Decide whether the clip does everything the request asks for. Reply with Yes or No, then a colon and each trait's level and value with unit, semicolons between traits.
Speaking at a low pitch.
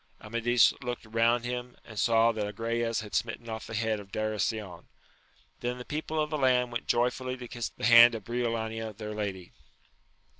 Yes: low, 115 Hz